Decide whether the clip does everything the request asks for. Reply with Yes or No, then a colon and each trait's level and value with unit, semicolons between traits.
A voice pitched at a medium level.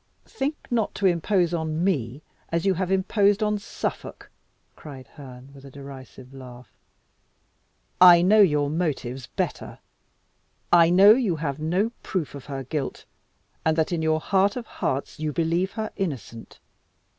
Yes: medium, 165 Hz